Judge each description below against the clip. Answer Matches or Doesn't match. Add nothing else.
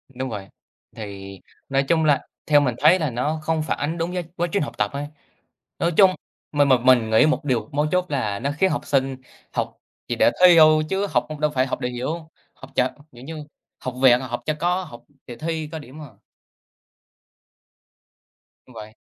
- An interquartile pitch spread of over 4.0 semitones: Matches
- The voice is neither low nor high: Matches